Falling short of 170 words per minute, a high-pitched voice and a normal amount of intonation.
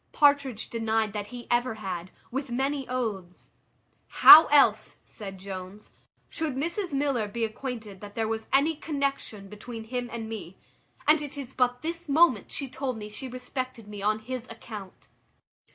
Yes: average, 160 wpm; high, 240 Hz; average, 4.6 semitones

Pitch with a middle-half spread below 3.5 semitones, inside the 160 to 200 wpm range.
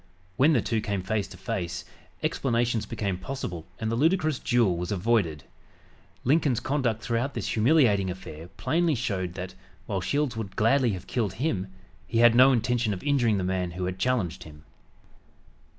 No: wide, 5.4 semitones; average, 165 wpm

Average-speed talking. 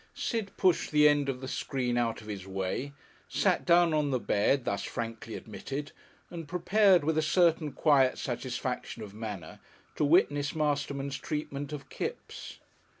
Yes: average, 155 wpm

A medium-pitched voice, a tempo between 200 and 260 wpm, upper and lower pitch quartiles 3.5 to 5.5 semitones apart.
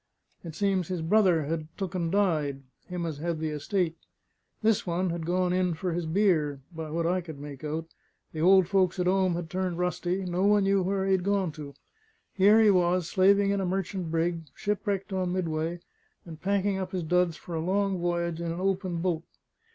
No: medium, 180 Hz; fast, 205 wpm; narrow, 2.6 semitones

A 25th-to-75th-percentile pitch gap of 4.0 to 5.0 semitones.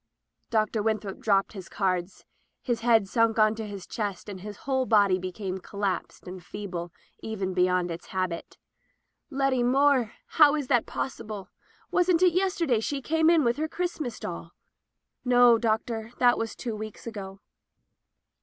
Yes: average, 4.7 semitones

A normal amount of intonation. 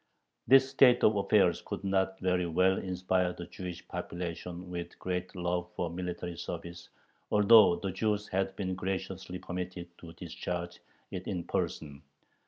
No: narrow, 1.5 semitones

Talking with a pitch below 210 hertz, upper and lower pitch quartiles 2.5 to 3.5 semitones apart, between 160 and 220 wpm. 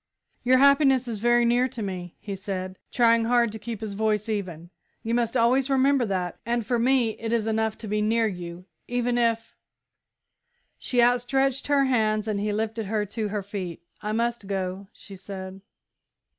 No: high, 220 Hz; average, 3.1 semitones; average, 185 wpm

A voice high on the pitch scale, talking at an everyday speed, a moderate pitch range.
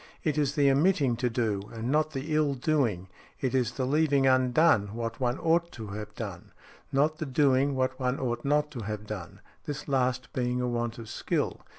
No: low, 130 Hz; average, 185 wpm; average, 3.8 semitones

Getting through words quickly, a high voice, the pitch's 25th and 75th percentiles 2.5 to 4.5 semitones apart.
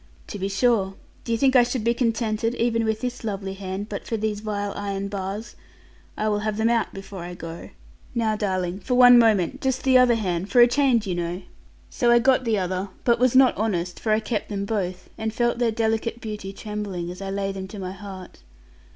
Yes: fast, 220 wpm; high, 215 Hz; average, 3.3 semitones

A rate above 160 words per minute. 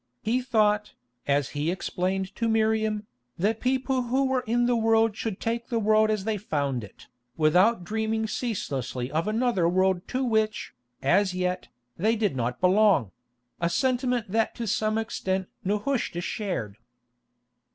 No: average, 150 wpm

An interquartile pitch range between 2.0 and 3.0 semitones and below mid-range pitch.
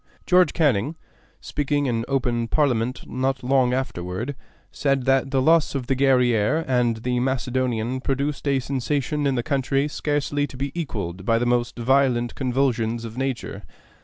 Yes: narrow, 2.6 semitones; low, 130 Hz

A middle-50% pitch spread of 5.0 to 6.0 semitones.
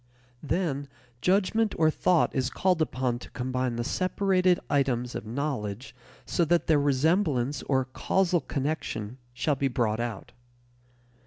Yes: wide, 5.6 semitones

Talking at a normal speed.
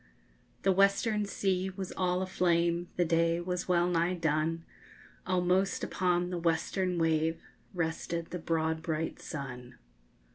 No: slow, 130 wpm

